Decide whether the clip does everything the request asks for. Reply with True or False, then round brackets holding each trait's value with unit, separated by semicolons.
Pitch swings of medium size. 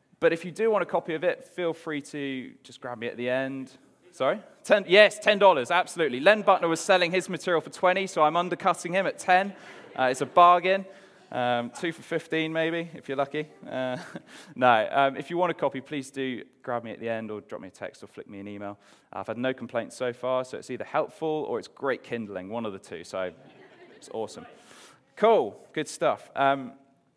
False (6.0 semitones)